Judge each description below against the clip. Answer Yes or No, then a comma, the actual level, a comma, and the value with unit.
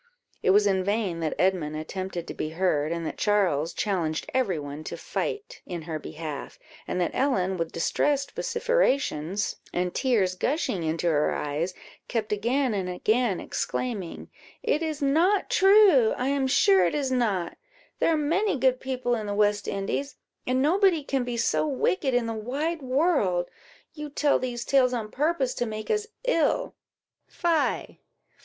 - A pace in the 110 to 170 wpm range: Yes, average, 165 wpm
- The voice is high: Yes, high, 230 Hz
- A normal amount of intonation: No, wide, 7.7 semitones